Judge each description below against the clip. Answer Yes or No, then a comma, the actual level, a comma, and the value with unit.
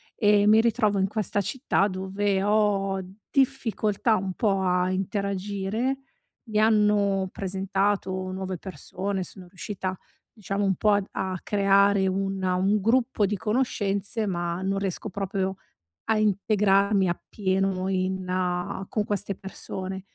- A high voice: Yes, high, 195 Hz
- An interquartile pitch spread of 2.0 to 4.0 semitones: No, narrow, 1.6 semitones